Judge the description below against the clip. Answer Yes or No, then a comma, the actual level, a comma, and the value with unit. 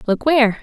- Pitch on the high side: Yes, very high, 250 Hz